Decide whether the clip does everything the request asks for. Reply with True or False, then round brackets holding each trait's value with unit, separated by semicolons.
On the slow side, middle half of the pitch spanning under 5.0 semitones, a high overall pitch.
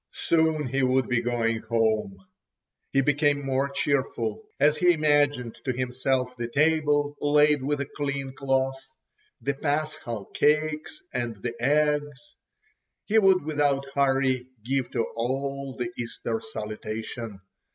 False (130 wpm; 3.1 semitones; 135 Hz)